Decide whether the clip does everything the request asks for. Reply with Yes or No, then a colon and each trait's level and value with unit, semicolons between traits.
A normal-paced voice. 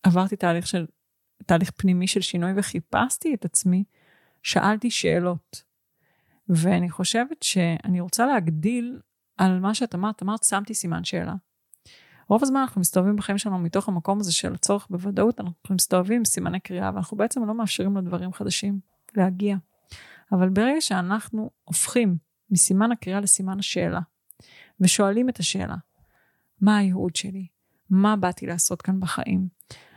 Yes: average, 135 wpm